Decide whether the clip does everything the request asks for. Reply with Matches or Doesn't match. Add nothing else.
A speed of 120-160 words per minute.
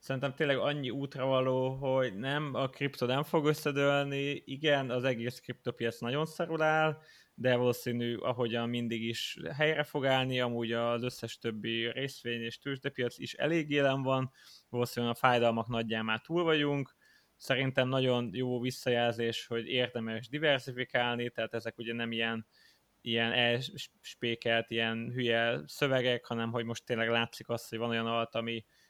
Matches